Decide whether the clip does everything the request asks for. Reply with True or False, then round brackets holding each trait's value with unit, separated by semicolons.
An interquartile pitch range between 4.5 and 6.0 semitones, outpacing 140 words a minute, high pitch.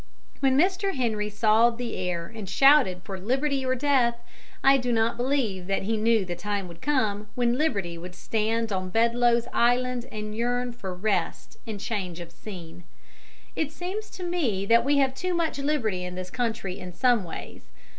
True (5.1 semitones; 180 wpm; 230 Hz)